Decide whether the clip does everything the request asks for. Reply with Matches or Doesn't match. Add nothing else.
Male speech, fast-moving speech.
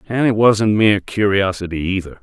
Doesn't match